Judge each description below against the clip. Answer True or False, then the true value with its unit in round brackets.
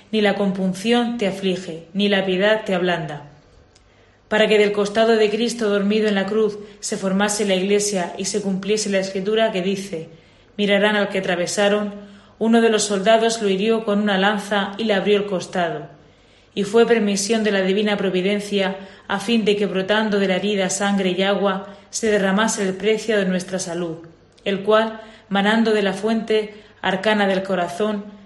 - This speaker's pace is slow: False (175 wpm)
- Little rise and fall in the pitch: True (2.0 semitones)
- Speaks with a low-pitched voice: False (205 Hz)